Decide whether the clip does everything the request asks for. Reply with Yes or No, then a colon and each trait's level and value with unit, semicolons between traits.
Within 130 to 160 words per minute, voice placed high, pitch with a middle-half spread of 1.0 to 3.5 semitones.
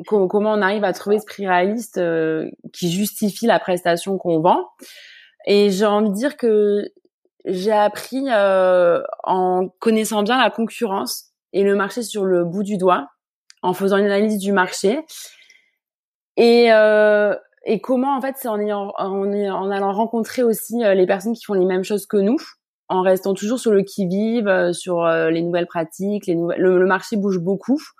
No: average, 180 wpm; high, 200 Hz; average, 3.1 semitones